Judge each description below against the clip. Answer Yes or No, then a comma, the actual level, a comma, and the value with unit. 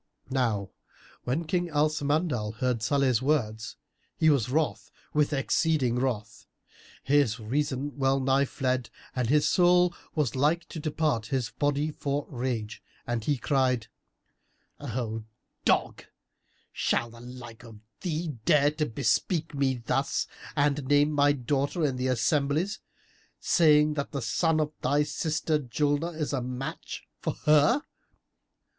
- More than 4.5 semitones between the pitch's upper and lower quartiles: No, average, 3.4 semitones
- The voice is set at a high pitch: No, medium, 140 Hz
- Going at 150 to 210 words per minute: No, slow, 135 wpm